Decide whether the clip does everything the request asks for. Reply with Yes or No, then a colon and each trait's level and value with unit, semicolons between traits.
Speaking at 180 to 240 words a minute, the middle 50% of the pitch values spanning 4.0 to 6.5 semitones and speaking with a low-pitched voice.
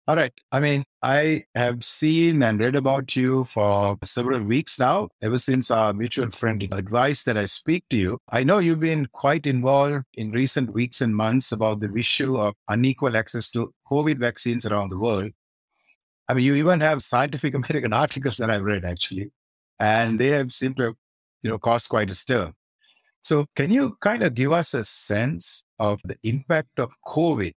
Yes: average, 195 wpm; average, 4.4 semitones; low, 125 Hz